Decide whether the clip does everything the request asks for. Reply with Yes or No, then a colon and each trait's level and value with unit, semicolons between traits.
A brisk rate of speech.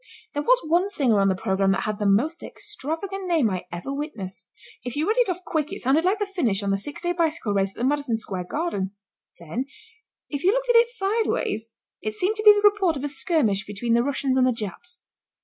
Yes: fast, 235 wpm